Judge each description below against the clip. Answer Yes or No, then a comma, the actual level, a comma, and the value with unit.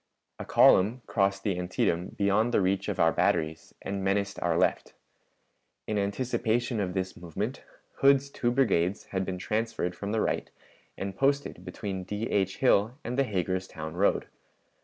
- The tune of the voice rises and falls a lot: No, average, 3.5 semitones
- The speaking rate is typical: Yes, average, 160 wpm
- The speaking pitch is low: Yes, low, 100 Hz